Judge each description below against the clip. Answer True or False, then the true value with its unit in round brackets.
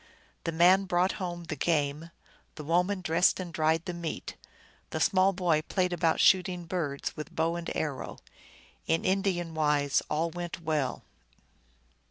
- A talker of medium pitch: True (170 Hz)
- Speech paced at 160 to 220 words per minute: False (150 wpm)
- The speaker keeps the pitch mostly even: True (2.3 semitones)